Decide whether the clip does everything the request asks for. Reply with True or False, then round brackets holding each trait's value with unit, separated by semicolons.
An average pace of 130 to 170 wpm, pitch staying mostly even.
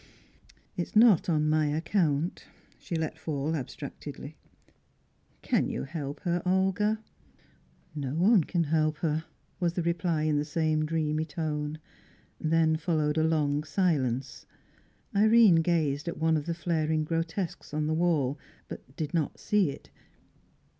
True (140 wpm; 2.2 semitones)